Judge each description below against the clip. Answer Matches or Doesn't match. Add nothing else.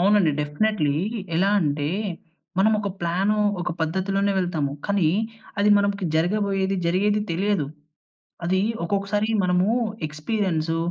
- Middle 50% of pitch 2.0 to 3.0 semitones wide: Doesn't match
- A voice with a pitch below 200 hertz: Matches